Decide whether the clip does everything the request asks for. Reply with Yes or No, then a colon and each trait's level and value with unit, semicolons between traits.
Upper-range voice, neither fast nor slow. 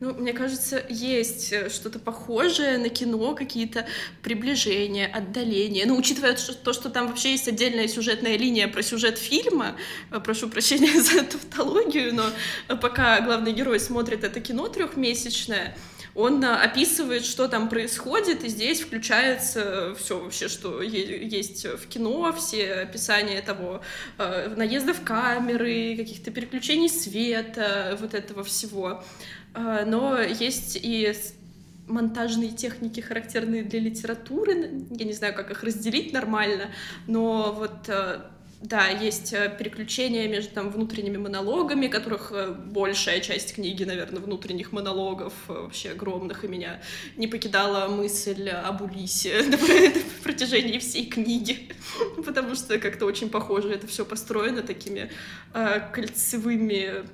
Yes: high, 225 Hz; average, 125 wpm